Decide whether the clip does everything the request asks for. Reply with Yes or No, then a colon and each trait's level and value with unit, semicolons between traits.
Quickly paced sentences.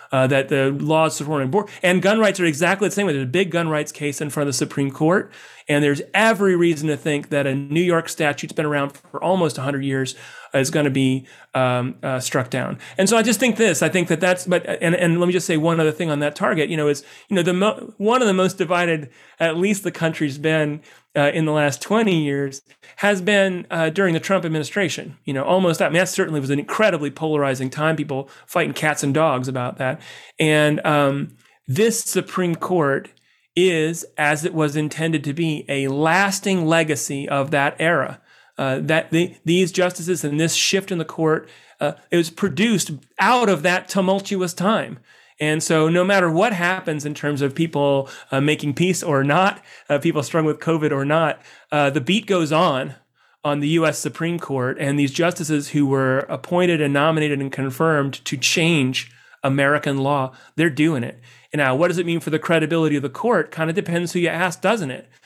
Yes: fast, 210 wpm